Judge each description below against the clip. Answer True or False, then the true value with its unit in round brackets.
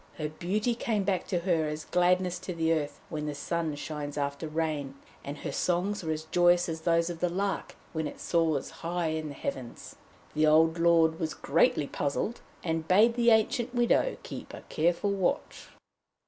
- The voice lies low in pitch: False (165 Hz)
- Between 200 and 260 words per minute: False (185 wpm)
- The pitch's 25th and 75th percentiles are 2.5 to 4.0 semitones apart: True (2.8 semitones)